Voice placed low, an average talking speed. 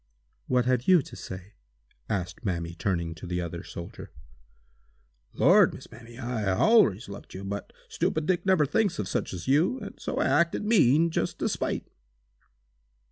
Yes: low, 120 Hz; average, 165 wpm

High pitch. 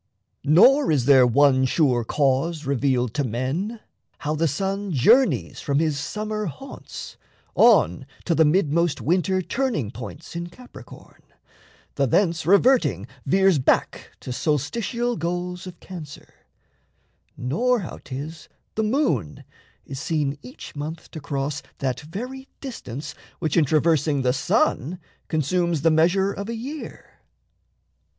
No: medium, 160 Hz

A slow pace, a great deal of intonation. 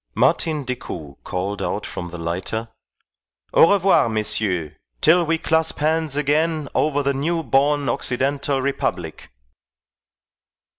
Yes: slow, 115 wpm; wide, 6.2 semitones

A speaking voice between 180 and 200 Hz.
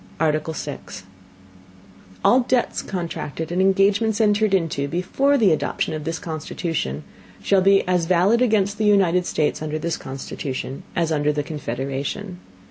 No: medium, 170 Hz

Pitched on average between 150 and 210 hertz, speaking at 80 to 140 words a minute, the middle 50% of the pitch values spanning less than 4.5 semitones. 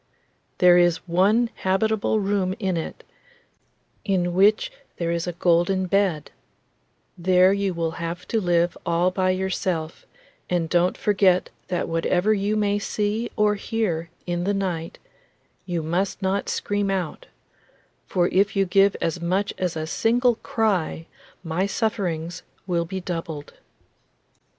Yes: medium, 185 Hz; slow, 135 wpm; average, 2.7 semitones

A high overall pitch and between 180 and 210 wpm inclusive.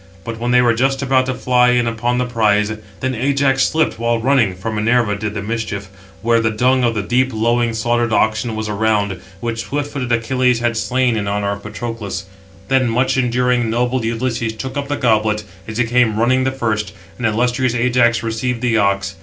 No: low, 115 Hz; average, 200 wpm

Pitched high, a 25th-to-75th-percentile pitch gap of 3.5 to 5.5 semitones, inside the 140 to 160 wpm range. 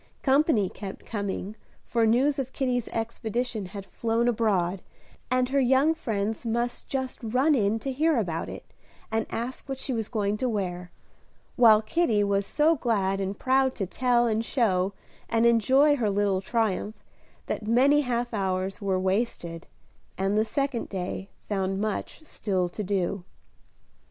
Yes: high, 225 Hz; average, 4.2 semitones; average, 155 wpm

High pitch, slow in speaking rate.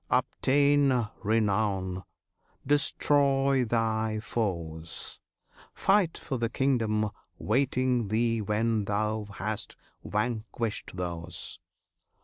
No: low, 110 Hz; slow, 80 wpm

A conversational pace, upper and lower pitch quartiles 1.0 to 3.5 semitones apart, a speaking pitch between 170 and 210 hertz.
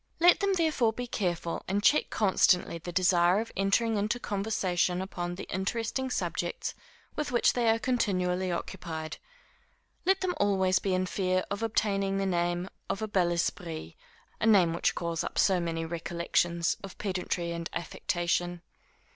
No: average, 155 wpm; average, 3.9 semitones; high, 190 Hz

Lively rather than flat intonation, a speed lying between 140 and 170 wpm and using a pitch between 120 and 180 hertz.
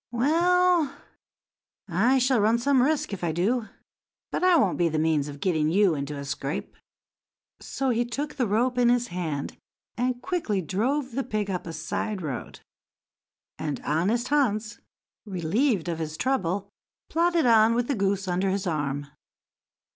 No: wide, 7.1 semitones; average, 160 wpm; high, 210 Hz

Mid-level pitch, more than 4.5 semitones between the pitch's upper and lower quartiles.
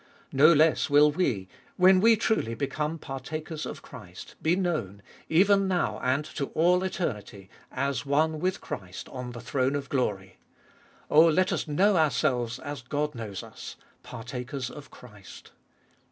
Yes: medium, 145 Hz; average, 4.9 semitones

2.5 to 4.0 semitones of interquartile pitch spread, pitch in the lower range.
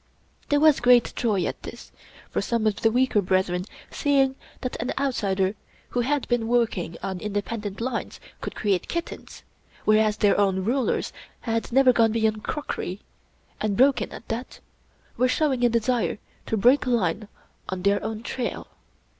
No: average, 3.7 semitones; high, 225 Hz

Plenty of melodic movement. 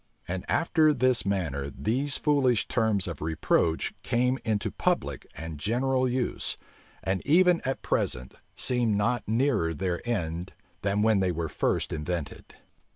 Yes: wide, 7.2 semitones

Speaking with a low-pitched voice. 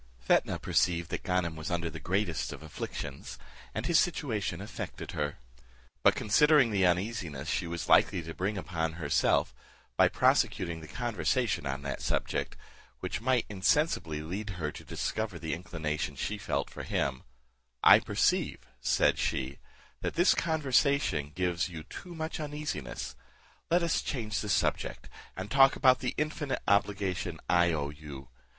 Yes: very low, 90 Hz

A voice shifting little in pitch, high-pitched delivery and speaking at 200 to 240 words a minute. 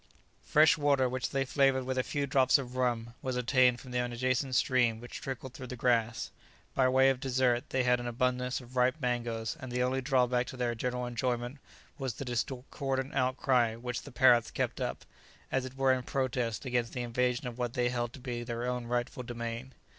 No: narrow, 1.3 semitones; low, 125 Hz; fast, 205 wpm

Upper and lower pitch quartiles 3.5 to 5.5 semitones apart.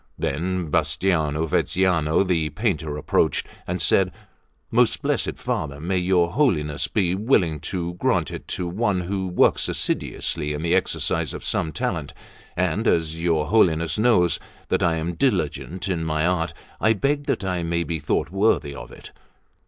No: average, 3.1 semitones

